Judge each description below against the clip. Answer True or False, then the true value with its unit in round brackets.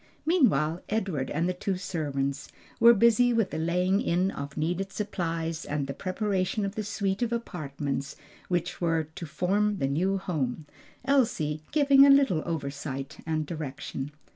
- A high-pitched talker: False (175 Hz)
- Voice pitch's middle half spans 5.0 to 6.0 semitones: True (5.3 semitones)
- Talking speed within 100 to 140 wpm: False (155 wpm)